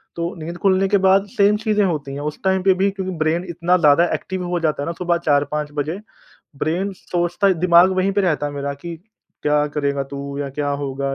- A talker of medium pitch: Yes, medium, 170 Hz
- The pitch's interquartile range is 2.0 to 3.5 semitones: No, average, 4.4 semitones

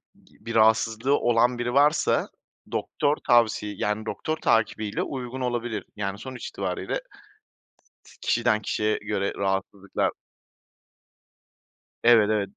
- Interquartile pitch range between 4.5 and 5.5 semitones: No, average, 2.7 semitones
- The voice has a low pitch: Yes, low, 115 Hz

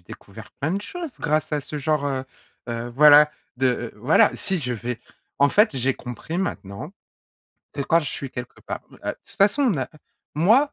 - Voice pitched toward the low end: No, medium, 145 Hz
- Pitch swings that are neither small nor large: No, wide, 6.0 semitones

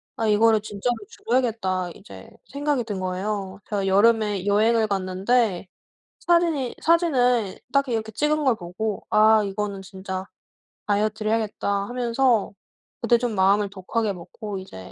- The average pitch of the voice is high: Yes, high, 215 Hz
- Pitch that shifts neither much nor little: Yes, average, 3.6 semitones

